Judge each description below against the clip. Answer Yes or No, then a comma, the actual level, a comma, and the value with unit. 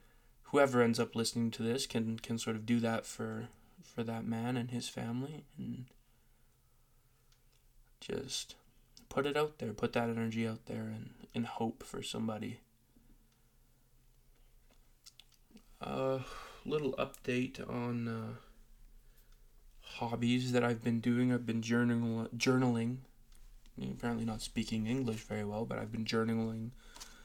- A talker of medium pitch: No, low, 120 Hz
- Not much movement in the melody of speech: Yes, narrow, 1.5 semitones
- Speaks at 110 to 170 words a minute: Yes, slow, 135 wpm